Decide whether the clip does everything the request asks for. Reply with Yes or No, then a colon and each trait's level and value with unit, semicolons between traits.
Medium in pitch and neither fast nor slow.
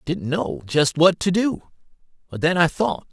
No: medium, 165 Hz; fast, 210 wpm